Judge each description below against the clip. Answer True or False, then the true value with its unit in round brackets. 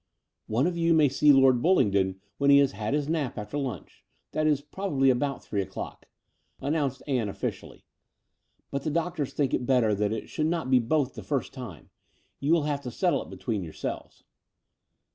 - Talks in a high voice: False (135 Hz)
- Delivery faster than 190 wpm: True (200 wpm)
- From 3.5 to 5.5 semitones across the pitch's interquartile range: True (4.1 semitones)